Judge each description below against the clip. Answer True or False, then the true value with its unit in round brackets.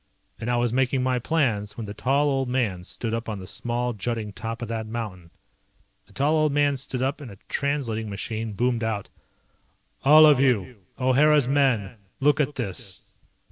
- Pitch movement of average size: True (3.9 semitones)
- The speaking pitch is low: True (120 Hz)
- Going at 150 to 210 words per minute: True (180 wpm)